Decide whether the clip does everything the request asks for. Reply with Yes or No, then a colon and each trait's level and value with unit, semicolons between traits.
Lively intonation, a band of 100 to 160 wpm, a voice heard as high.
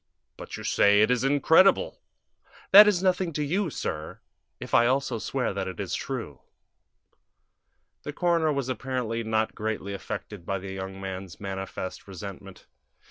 No: wide, 7.0 semitones; average, 150 wpm; low, 115 Hz